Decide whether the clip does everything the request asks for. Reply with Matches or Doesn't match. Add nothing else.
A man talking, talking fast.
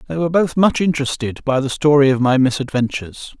Doesn't match